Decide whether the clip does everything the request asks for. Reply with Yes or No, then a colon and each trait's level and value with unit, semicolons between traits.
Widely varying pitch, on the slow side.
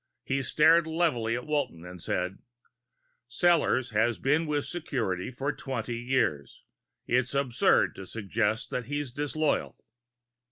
No: average, 4.6 semitones; slow, 125 wpm